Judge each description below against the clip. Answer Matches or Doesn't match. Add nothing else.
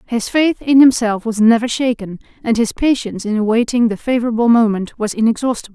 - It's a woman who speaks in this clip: Matches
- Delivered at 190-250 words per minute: Doesn't match